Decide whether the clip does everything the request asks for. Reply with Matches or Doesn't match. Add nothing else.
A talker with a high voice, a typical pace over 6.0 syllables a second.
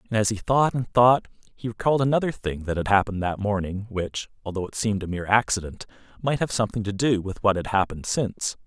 Doesn't match